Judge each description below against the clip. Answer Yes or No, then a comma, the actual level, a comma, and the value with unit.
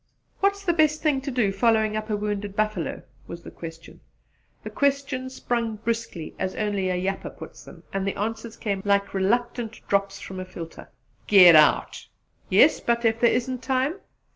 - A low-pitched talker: No, high, 215 Hz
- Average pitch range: Yes, average, 4.0 semitones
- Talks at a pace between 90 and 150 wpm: No, average, 175 wpm